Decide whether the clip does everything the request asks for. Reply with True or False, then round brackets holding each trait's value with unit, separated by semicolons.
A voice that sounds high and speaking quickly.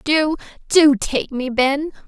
False (285 Hz; 145 wpm)